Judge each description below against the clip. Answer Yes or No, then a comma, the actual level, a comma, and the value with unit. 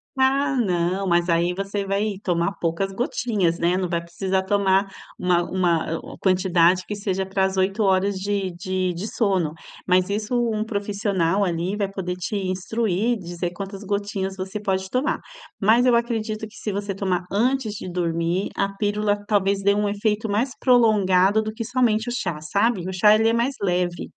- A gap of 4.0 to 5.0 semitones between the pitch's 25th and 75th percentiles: No, average, 2.7 semitones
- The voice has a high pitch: Yes, high, 195 Hz